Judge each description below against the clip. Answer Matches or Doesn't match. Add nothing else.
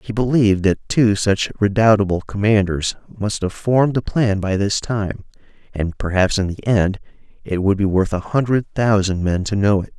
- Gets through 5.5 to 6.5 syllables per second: Doesn't match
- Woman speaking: Doesn't match